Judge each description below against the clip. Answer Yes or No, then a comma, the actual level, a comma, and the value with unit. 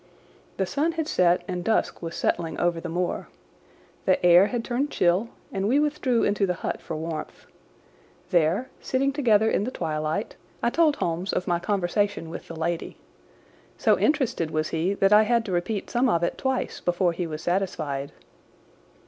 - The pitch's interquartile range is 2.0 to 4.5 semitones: No, wide, 5.5 semitones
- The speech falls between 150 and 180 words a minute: Yes, average, 175 wpm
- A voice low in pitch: No, medium, 185 Hz